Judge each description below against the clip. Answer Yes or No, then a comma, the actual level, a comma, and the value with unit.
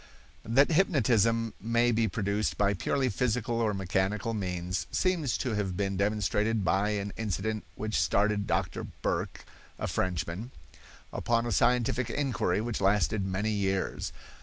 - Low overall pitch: Yes, low, 105 Hz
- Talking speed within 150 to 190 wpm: No, slow, 135 wpm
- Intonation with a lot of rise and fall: No, average, 3.0 semitones